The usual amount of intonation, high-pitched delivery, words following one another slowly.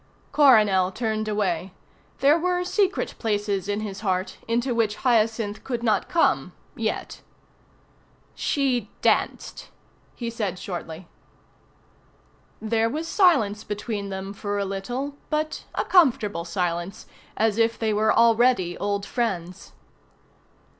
Yes: average, 3.6 semitones; high, 215 Hz; slow, 120 wpm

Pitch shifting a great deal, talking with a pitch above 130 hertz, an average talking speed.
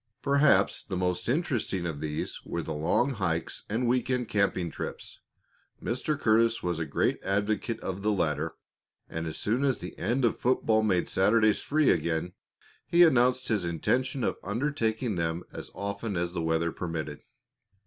No: wide, 6.4 semitones; low, 105 Hz; average, 165 wpm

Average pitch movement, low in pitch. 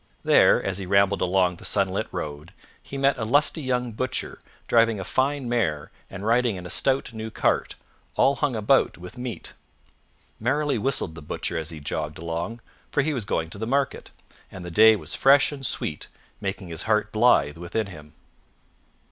No: wide, 6.1 semitones; low, 105 Hz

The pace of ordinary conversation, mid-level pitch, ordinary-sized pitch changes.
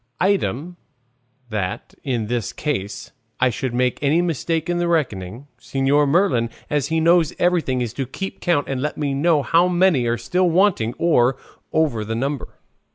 No: average, 160 wpm; medium, 145 Hz; wide, 5.8 semitones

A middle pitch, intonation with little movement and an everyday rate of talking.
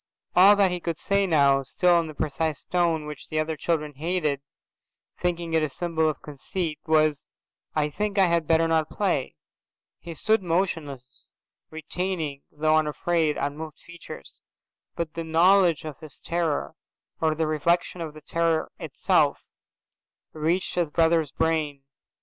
Yes: medium, 160 Hz; narrow, 2.2 semitones; average, 145 wpm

